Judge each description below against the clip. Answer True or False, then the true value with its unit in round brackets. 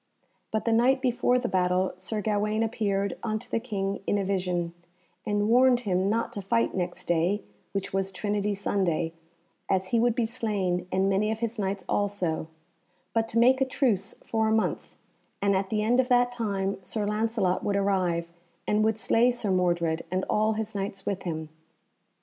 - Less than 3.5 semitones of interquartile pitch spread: True (3.0 semitones)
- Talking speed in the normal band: True (185 wpm)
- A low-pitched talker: False (205 Hz)